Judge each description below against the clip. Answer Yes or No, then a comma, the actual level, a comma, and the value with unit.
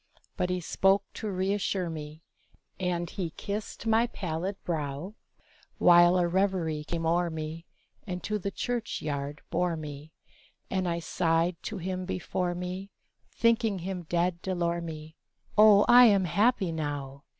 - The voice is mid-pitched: Yes, medium, 175 Hz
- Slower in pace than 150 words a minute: Yes, average, 140 wpm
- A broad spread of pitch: No, average, 3.0 semitones